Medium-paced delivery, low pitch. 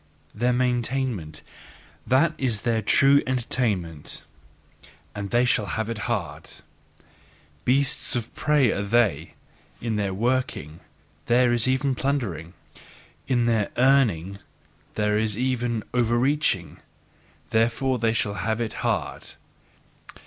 No: slow, 115 wpm; low, 120 Hz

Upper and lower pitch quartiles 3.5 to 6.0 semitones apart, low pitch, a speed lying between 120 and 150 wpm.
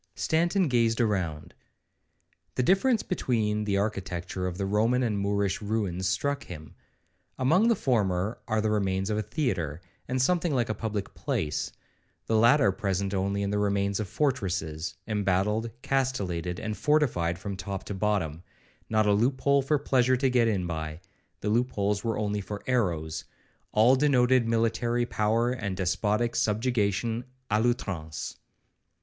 Yes: average, 4.2 semitones; low, 105 Hz; average, 145 wpm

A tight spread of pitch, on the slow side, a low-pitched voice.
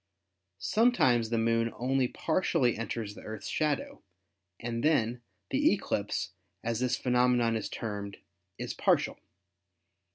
Yes: narrow, 2.1 semitones; slow, 125 wpm; low, 120 Hz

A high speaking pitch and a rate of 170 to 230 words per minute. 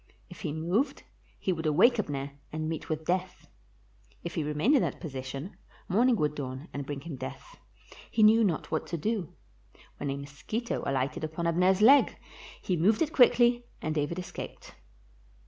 No: medium, 170 Hz; average, 175 wpm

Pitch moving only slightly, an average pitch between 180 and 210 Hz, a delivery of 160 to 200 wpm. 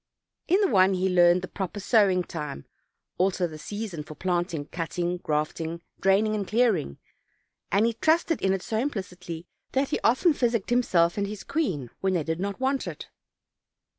No: average, 4.5 semitones; high, 190 Hz; average, 170 wpm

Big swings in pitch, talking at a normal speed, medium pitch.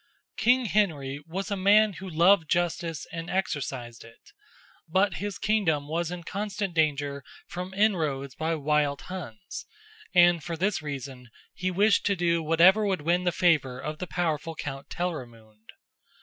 No: average, 4.4 semitones; average, 150 wpm; medium, 170 Hz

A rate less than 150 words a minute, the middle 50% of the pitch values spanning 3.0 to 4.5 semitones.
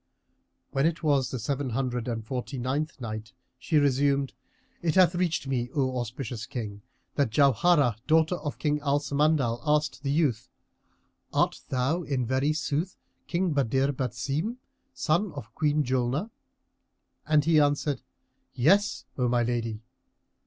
Yes: average, 140 wpm; average, 3.7 semitones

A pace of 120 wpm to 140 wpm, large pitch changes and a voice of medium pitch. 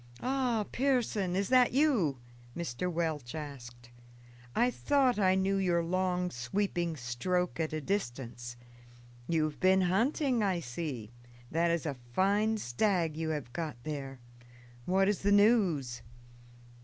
Yes: slow, 135 wpm; wide, 5.9 semitones; medium, 175 Hz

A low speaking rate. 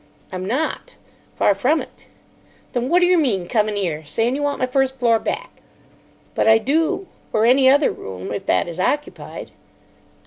No: average, 170 wpm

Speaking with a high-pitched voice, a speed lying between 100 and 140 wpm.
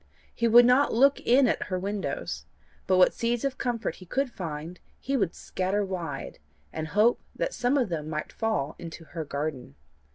No: high, 200 Hz; average, 185 wpm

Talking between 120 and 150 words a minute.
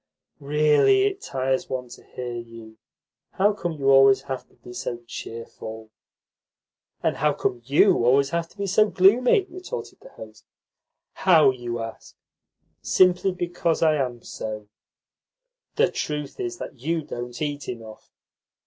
Yes: slow, 135 wpm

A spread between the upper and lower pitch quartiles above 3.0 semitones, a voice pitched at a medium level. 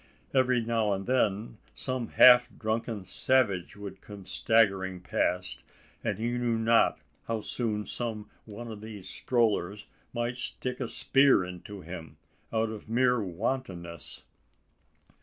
No: average, 3.7 semitones; low, 110 Hz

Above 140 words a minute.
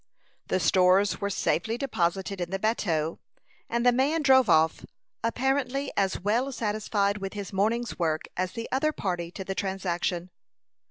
Yes: average, 155 wpm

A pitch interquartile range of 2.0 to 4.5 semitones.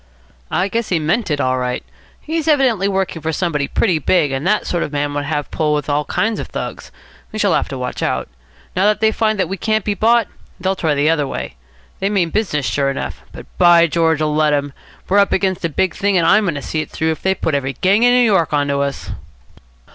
No: wide, 5.5 semitones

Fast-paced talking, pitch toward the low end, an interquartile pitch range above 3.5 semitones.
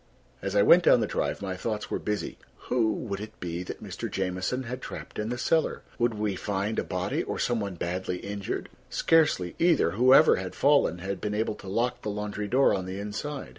Yes: fast, 210 wpm; low, 105 Hz; average, 4.2 semitones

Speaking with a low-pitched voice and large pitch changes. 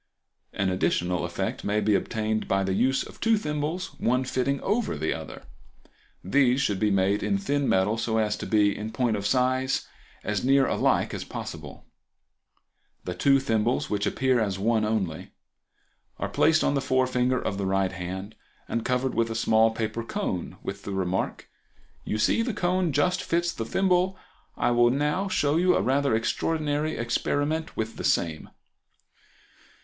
Yes: low, 120 Hz; wide, 5.7 semitones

